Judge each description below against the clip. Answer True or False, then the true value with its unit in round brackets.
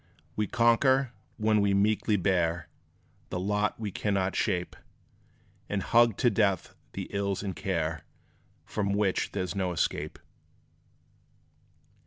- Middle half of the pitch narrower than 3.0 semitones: True (2.4 semitones)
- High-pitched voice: False (100 Hz)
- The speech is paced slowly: True (125 wpm)